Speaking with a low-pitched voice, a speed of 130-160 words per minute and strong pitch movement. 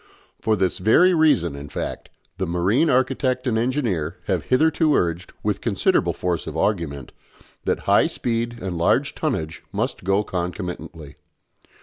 Yes: very low, 95 Hz; average, 140 wpm; wide, 7.0 semitones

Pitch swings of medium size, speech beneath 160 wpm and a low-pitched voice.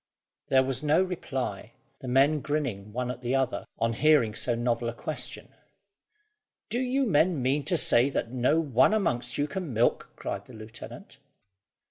No: average, 4.4 semitones; average, 165 wpm; low, 130 Hz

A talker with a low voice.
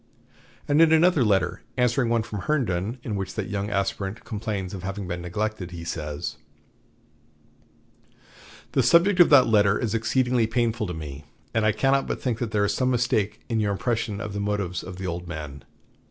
Yes: low, 105 Hz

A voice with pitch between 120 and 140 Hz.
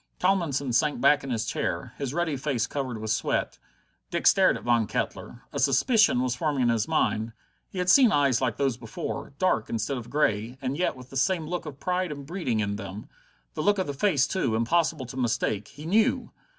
Yes: low, 135 Hz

